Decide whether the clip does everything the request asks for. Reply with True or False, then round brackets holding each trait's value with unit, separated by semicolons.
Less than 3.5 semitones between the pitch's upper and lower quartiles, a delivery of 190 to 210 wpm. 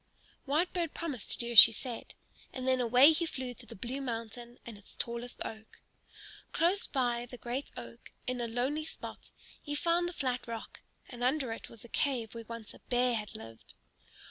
True (3.0 semitones; 195 wpm)